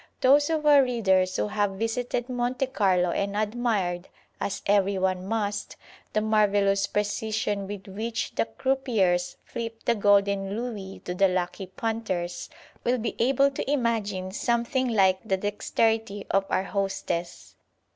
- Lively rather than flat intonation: No, average, 3.4 semitones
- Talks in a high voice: Yes, high, 205 Hz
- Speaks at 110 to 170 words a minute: Yes, average, 140 wpm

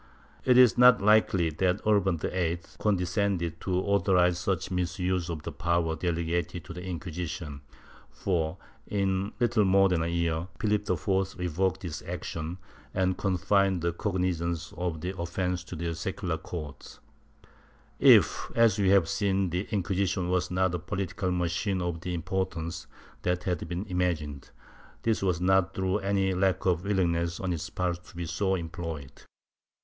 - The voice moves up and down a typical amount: No, narrow, 2.2 semitones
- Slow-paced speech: No, average, 155 wpm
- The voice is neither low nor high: No, very low, 90 Hz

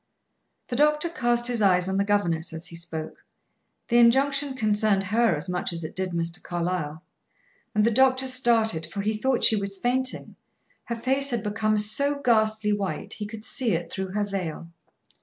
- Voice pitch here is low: No, high, 210 Hz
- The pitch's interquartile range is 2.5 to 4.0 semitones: No, average, 4.8 semitones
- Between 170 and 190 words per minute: Yes, average, 180 wpm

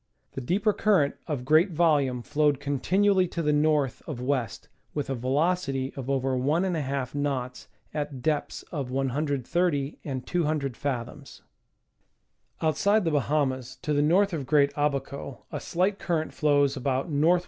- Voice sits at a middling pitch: Yes, medium, 145 Hz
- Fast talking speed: No, average, 155 wpm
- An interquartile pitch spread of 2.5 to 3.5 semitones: Yes, average, 3.2 semitones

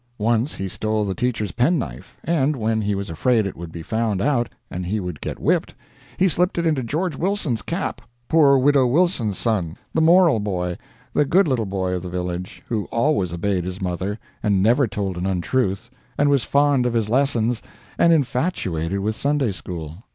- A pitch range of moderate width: No, wide, 6.8 semitones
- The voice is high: No, low, 110 Hz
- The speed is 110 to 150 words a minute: No, average, 190 wpm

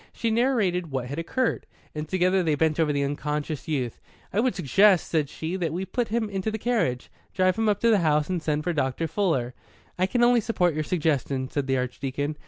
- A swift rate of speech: Yes, fast, 215 wpm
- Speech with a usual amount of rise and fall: No, wide, 5.7 semitones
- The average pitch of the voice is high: No, medium, 165 Hz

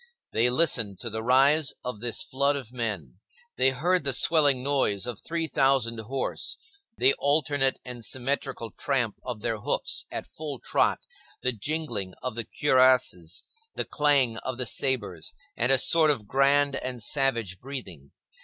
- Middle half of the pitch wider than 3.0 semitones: Yes, average, 3.8 semitones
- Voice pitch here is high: No, low, 130 Hz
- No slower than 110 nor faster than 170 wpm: Yes, average, 155 wpm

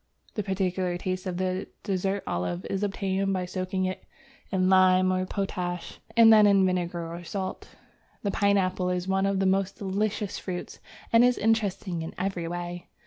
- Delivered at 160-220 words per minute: Yes, average, 170 wpm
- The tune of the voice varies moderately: No, narrow, 1.5 semitones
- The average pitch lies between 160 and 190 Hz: Yes, medium, 185 Hz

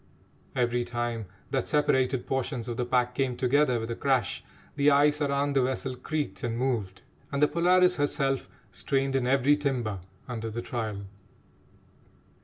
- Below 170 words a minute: Yes, average, 155 wpm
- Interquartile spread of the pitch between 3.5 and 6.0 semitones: No, average, 2.9 semitones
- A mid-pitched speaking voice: No, low, 130 Hz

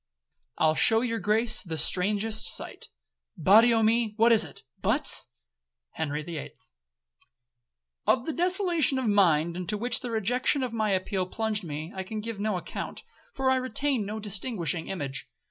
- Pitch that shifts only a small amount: No, average, 4.2 semitones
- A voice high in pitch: Yes, high, 215 Hz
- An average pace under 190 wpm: Yes, average, 160 wpm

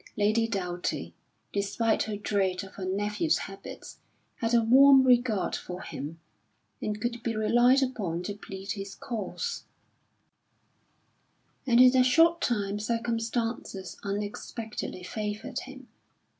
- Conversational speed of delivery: No, slow, 120 wpm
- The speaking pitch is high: Yes, high, 215 Hz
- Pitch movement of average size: Yes, average, 3.4 semitones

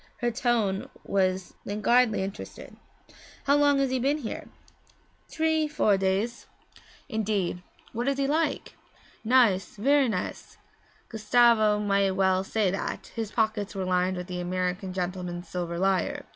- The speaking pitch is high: Yes, high, 210 Hz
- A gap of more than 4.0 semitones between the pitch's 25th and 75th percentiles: Yes, average, 4.5 semitones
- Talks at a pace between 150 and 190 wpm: No, slow, 135 wpm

